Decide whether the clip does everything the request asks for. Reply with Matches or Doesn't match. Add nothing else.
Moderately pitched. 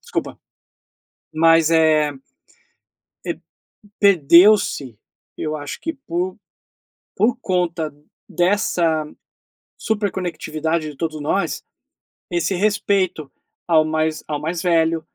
Matches